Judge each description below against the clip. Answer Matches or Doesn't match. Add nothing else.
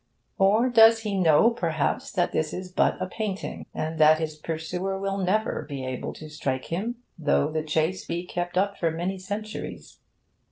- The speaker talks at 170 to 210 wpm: Matches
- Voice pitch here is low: Doesn't match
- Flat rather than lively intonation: Doesn't match